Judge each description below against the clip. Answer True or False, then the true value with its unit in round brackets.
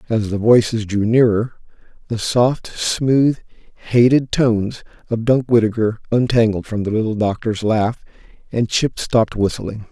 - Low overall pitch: True (115 Hz)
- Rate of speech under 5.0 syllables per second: True (4.3 syllables/s)